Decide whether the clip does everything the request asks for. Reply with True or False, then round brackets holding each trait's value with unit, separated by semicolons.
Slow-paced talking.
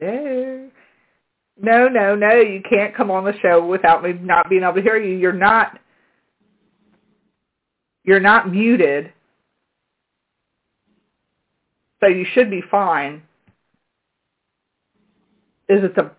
True (115 wpm)